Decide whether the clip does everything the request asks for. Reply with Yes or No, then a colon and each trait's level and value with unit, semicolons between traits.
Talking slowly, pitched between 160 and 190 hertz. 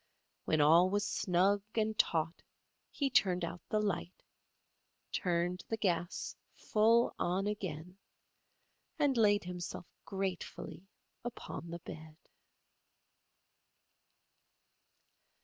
Yes: slow, 95 wpm; medium, 185 Hz